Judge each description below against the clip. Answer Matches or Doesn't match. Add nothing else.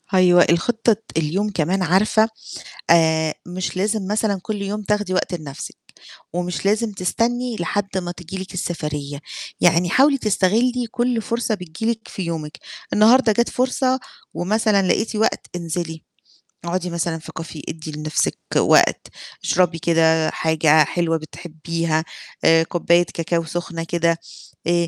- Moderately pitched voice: Matches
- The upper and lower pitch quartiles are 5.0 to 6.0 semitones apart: Doesn't match